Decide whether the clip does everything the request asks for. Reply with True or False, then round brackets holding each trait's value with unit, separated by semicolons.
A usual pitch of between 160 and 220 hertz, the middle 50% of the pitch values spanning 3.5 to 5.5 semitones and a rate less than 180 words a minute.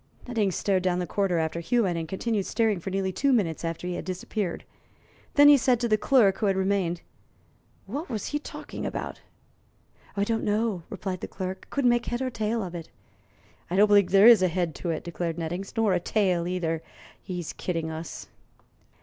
False (190 Hz; 4.1 semitones; 195 wpm)